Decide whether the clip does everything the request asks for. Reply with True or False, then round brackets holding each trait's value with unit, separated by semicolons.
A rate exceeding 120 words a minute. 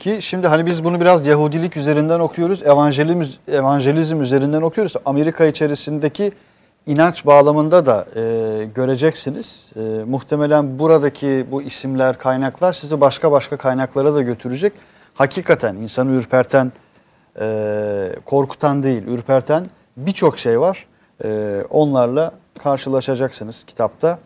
False (110 wpm)